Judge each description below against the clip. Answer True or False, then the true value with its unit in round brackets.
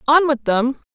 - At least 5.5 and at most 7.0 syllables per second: False (4.3 syllables/s)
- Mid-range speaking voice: False (270 Hz)